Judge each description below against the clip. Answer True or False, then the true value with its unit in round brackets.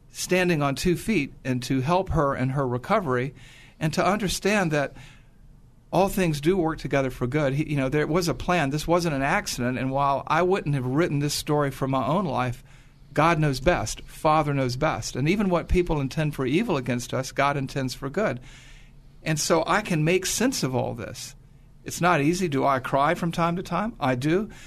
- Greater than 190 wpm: True (205 wpm)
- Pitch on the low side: False (145 Hz)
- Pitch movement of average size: True (4.4 semitones)